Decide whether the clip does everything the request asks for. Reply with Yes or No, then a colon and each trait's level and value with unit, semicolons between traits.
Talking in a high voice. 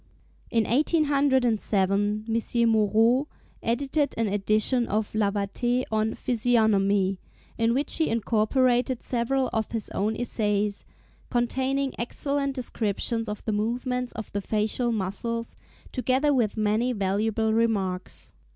Yes: high, 225 Hz